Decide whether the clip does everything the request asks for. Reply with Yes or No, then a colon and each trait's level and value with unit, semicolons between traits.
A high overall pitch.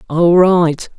No: medium, 170 Hz